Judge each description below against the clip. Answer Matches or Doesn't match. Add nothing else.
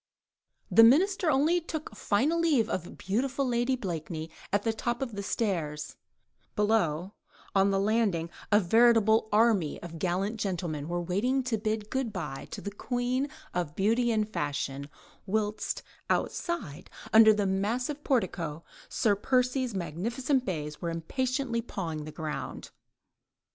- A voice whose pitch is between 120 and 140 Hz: Doesn't match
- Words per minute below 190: Matches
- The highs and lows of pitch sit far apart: Matches